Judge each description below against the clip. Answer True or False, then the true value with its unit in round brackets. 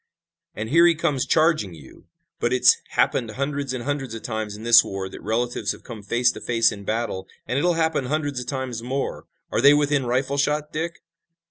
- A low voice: True (130 Hz)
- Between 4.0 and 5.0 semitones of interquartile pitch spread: True (4.3 semitones)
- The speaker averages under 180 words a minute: False (205 wpm)